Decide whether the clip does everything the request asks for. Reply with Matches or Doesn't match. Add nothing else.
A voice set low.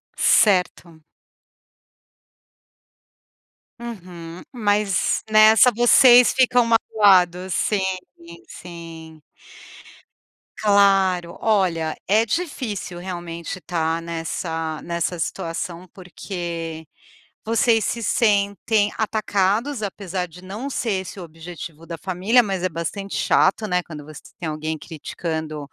Doesn't match